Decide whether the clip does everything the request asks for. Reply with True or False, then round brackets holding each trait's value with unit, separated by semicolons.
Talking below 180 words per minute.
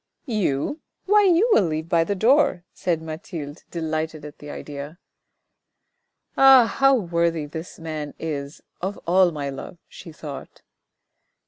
True (140 wpm)